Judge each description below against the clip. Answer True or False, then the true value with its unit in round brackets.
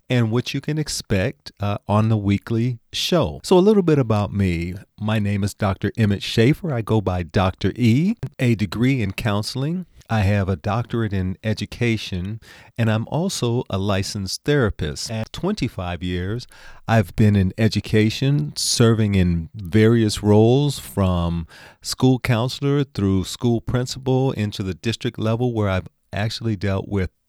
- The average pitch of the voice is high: False (110 Hz)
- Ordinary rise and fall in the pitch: True (3.9 semitones)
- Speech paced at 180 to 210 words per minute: False (150 wpm)